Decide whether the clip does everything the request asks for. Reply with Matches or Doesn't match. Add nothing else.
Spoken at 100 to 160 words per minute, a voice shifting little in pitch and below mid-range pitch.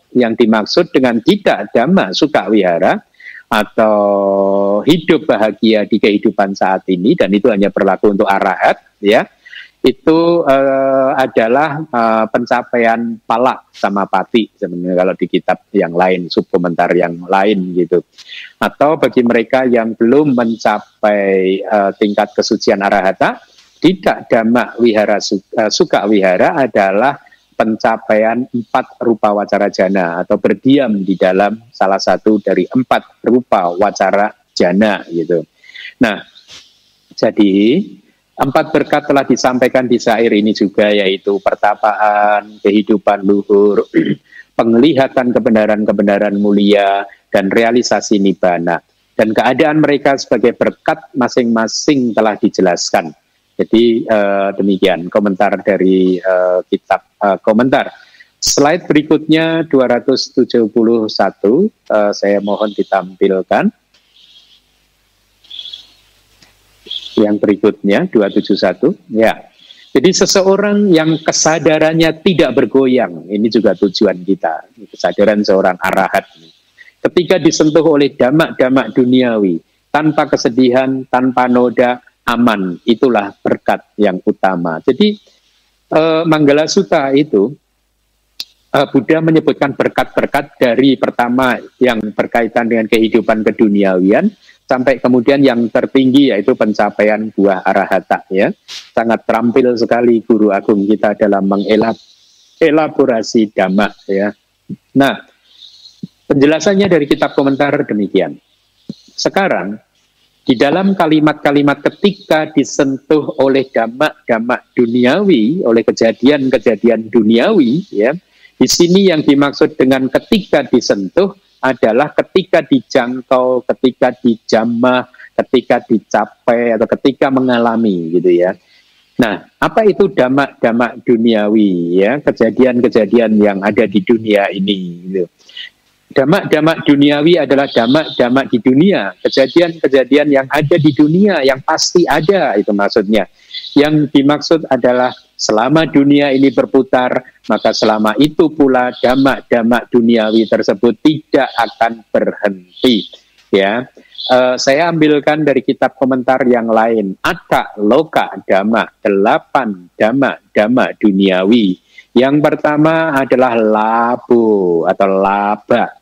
Doesn't match